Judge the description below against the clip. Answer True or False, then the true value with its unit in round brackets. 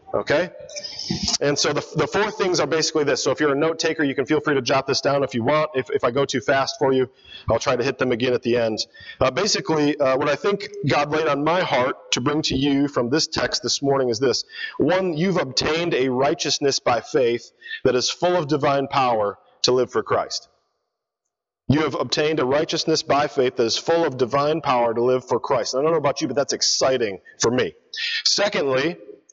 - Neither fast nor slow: False (230 wpm)